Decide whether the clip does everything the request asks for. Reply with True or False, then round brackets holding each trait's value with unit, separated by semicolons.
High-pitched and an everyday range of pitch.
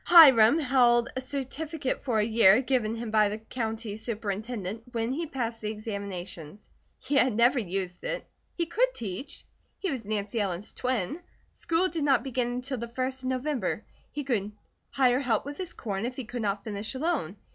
True (240 Hz; 4.1 semitones)